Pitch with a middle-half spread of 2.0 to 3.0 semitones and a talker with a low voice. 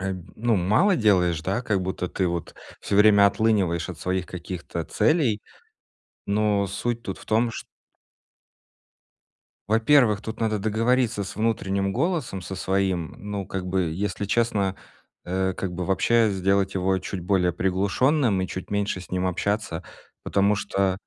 Yes: average, 2.7 semitones; low, 100 Hz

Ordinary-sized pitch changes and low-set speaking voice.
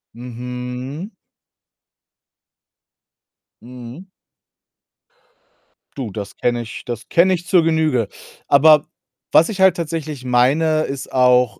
Yes: average, 4.4 semitones; low, 130 Hz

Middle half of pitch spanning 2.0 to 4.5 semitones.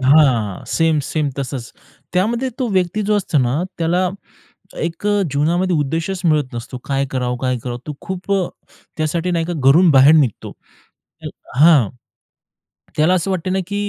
No: average, 5.1 semitones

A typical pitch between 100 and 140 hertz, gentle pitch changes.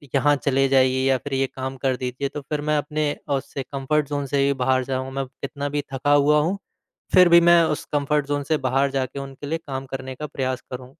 Yes: low, 135 Hz; narrow, 1.8 semitones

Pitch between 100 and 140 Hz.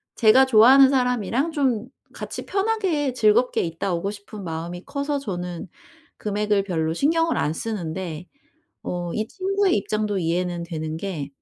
No: high, 210 Hz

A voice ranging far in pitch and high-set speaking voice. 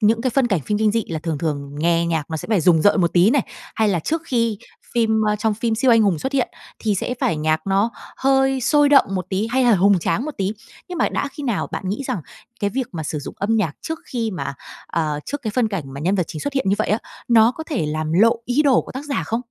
Yes: wide, 6.5 semitones; high, 215 Hz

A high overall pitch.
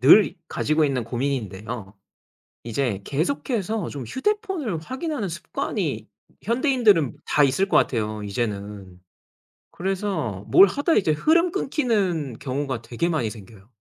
No: medium, 150 Hz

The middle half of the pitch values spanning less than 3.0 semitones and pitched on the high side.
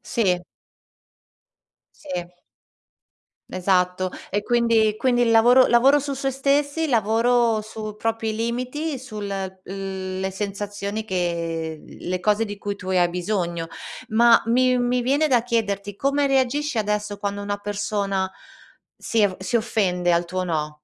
No: average, 4.3 semitones; high, 210 Hz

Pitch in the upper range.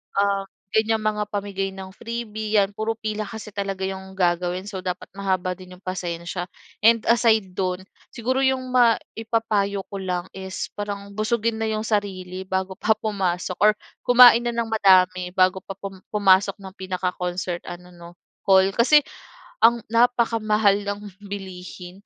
Yes: high, 200 Hz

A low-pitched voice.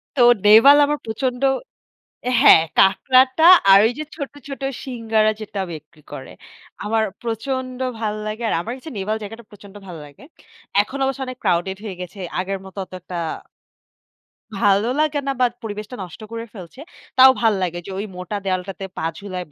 No: high, 215 Hz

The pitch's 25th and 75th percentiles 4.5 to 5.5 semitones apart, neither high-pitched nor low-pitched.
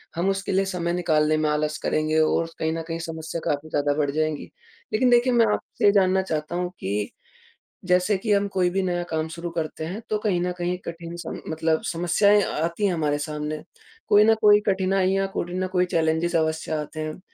No: average, 3.4 semitones; medium, 170 Hz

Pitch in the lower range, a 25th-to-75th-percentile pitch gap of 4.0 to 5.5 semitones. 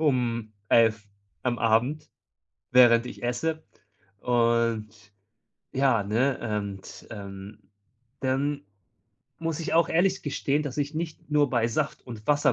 Yes: low, 125 Hz; average, 4.6 semitones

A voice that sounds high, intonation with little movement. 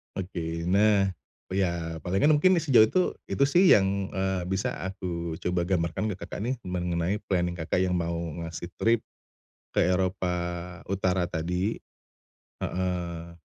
No: very low, 90 Hz; narrow, 2.2 semitones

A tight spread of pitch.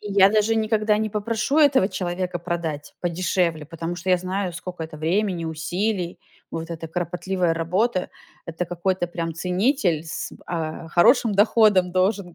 No: average, 3.6 semitones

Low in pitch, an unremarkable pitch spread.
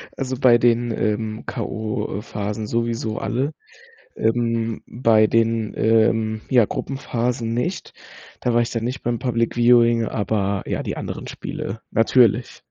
No: low, 115 Hz; narrow, 1.5 semitones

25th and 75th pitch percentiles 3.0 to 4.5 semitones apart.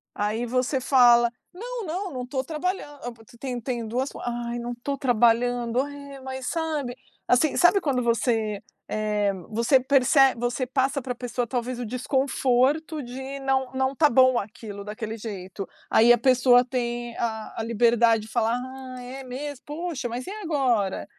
No: narrow, 2.5 semitones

